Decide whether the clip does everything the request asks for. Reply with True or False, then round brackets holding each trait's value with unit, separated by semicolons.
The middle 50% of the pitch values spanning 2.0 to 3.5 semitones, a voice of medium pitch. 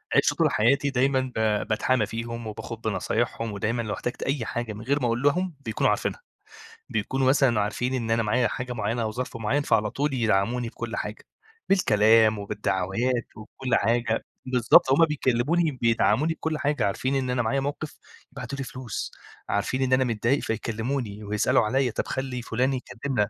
False (3.2 semitones; 120 Hz)